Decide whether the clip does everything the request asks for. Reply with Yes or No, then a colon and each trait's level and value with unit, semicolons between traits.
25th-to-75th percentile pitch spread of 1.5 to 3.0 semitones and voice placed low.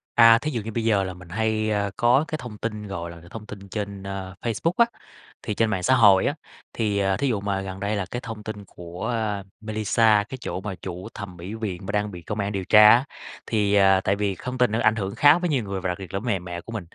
Yes: narrow, 2.6 semitones; low, 105 Hz